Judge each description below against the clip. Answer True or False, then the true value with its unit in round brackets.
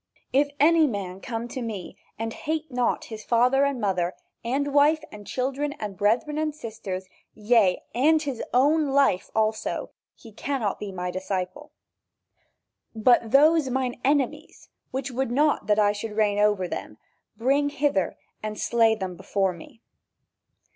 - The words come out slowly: False (150 wpm)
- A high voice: True (235 Hz)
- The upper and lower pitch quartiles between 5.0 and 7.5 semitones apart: True (5.3 semitones)